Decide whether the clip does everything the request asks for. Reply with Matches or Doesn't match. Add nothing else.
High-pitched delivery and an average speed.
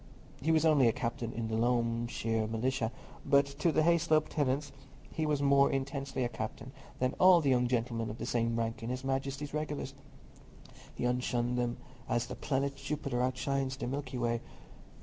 Doesn't match